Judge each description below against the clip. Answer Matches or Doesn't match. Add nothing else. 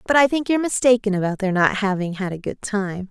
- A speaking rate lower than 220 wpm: Doesn't match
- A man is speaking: Doesn't match